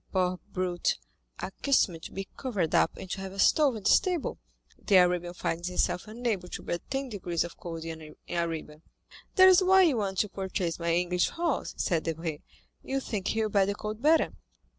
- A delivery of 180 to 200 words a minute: Yes, average, 185 wpm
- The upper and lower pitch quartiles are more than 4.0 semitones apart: Yes, average, 4.6 semitones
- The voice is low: No, high, 190 Hz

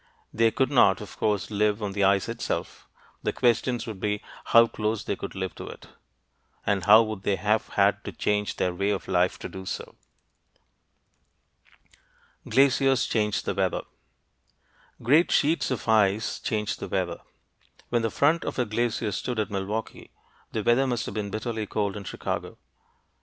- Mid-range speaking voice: No, low, 105 Hz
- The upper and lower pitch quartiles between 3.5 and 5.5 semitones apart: No, average, 2.8 semitones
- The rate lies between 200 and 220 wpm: No, average, 170 wpm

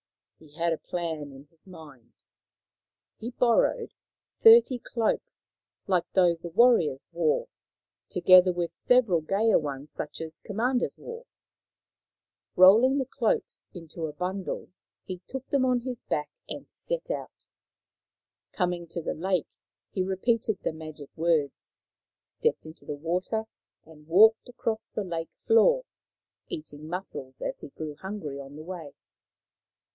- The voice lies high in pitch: No, medium, 180 Hz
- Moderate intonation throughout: No, wide, 6.2 semitones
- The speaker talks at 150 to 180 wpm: No, average, 140 wpm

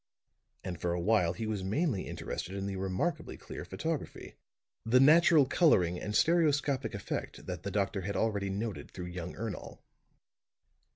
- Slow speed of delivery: No, average, 155 wpm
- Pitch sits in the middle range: No, low, 100 Hz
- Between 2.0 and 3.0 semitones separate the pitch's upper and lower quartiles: No, wide, 5.6 semitones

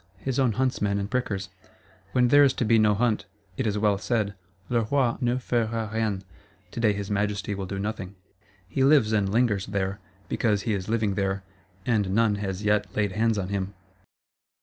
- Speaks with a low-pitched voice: Yes, low, 105 Hz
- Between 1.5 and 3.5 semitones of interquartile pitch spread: Yes, average, 2.7 semitones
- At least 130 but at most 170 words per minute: No, average, 185 wpm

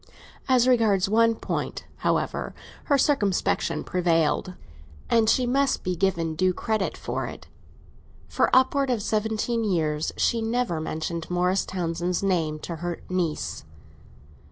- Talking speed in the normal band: No, slow, 130 wpm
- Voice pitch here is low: No, high, 190 Hz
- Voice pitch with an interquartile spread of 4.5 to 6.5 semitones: Yes, average, 5.1 semitones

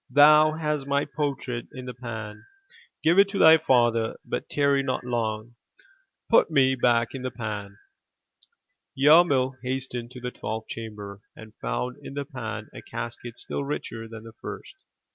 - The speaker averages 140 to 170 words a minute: Yes, average, 160 wpm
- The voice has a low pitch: Yes, low, 125 Hz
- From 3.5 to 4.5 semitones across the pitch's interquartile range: Yes, average, 3.8 semitones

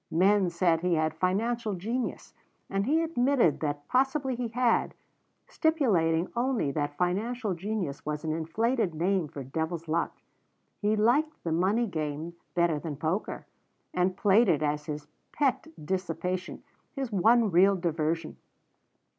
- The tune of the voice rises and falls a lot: Yes, wide, 6.3 semitones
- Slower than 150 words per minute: Yes, average, 140 wpm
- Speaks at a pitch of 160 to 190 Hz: Yes, medium, 185 Hz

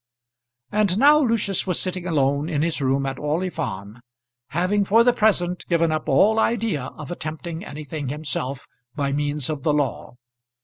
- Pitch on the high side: No, medium, 160 Hz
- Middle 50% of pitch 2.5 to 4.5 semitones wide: No, average, 5.1 semitones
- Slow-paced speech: No, average, 165 wpm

